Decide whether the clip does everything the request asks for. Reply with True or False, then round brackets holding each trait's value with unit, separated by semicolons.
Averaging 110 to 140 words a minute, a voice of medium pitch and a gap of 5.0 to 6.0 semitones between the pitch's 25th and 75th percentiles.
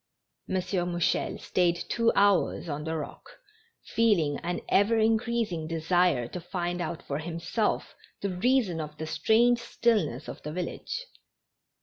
True (135 wpm; 175 Hz; 5.4 semitones)